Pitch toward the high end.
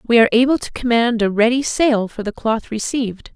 Yes: high, 230 Hz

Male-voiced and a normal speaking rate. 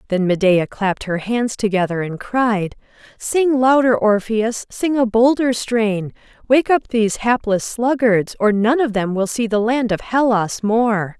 No: female; average, 165 wpm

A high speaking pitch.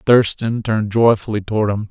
No: low, 110 Hz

